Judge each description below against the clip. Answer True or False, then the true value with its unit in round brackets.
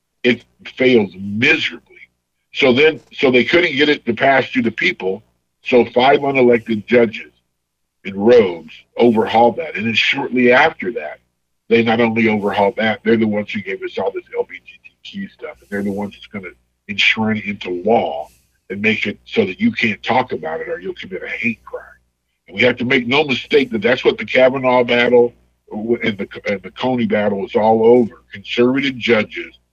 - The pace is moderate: True (190 wpm)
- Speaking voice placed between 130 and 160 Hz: False (115 Hz)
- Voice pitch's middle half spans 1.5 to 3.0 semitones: False (4.7 semitones)